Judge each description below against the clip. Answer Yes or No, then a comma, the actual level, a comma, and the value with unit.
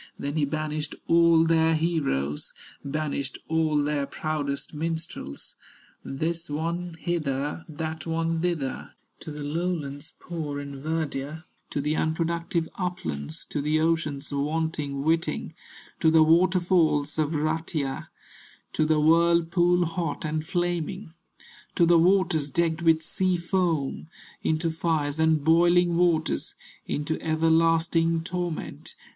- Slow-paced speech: Yes, slow, 120 wpm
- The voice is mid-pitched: Yes, medium, 160 Hz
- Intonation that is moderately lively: No, narrow, 2.1 semitones